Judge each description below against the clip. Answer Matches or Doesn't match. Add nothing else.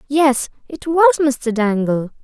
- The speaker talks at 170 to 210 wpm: Doesn't match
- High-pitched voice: Matches